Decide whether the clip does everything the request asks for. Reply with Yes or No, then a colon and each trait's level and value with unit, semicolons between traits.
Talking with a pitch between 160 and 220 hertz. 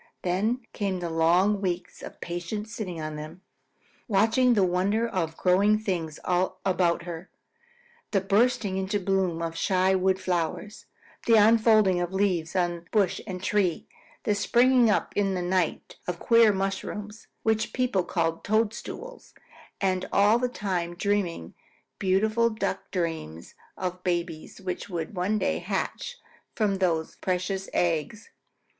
Yes: high, 190 Hz